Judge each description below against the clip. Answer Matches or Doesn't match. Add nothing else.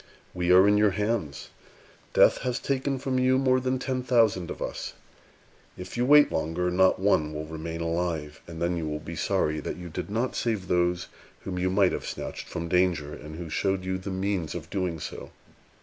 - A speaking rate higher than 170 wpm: Matches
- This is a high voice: Doesn't match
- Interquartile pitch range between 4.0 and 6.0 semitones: Matches